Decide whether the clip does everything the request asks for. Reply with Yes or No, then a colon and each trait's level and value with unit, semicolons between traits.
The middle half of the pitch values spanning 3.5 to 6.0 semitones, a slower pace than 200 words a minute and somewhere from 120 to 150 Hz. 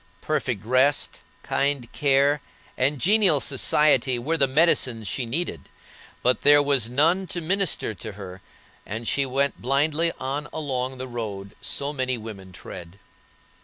Yes: average, 3.9 semitones; average, 145 wpm; low, 135 Hz